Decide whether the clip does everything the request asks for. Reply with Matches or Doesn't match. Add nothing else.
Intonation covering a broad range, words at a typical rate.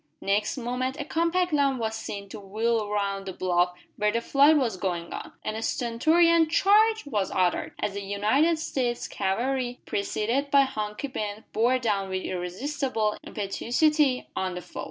Matches